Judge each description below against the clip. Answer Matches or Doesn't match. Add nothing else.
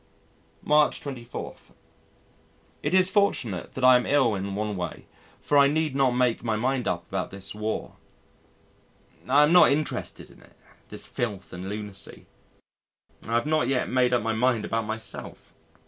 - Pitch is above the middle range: Doesn't match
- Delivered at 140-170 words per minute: Matches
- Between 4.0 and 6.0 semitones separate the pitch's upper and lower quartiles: Matches